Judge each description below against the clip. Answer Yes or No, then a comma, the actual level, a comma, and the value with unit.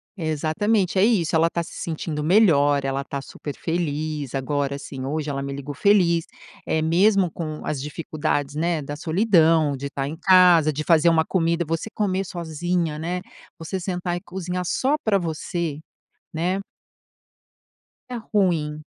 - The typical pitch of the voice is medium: Yes, medium, 165 Hz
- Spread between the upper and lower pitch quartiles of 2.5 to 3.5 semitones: Yes, average, 3.2 semitones